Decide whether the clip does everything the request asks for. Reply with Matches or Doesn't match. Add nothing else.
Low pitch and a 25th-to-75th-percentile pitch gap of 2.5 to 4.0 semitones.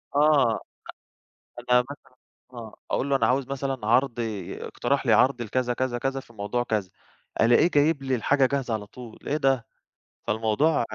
Matches